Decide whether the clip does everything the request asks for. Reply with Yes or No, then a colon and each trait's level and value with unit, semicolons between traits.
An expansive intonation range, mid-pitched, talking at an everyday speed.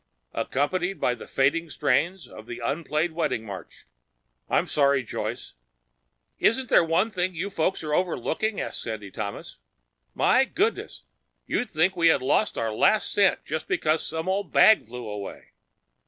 Yes: wide, 6.6 semitones; medium, 160 Hz; average, 155 wpm